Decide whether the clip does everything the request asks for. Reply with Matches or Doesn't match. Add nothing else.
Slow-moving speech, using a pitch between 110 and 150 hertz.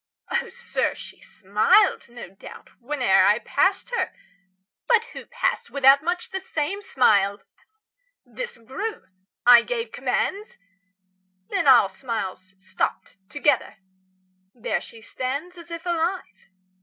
Doesn't match